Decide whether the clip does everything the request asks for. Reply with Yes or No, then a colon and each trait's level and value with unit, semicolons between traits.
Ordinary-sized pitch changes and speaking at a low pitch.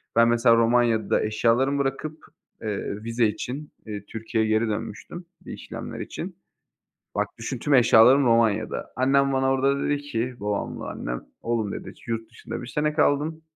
Yes: average, 3.6 semitones; low, 115 Hz